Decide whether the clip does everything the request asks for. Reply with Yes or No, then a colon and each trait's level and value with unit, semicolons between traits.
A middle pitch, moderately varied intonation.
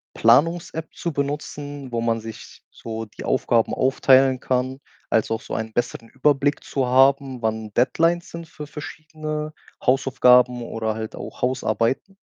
No: low, 130 Hz; average, 4.1 semitones